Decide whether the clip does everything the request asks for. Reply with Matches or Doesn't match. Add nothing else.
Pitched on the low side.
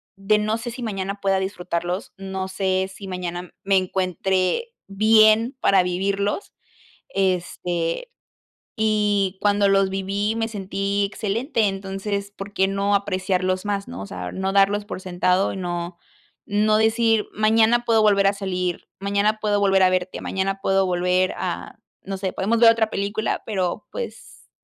Doesn't match